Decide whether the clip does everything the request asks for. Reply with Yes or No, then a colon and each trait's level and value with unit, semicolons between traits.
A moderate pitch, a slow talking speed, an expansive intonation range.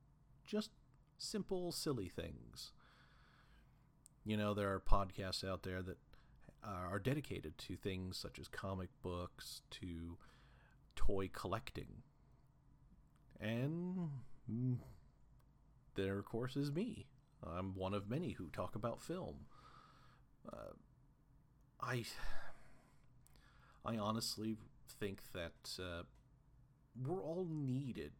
No: low, 125 Hz; slow, 100 wpm; wide, 6.1 semitones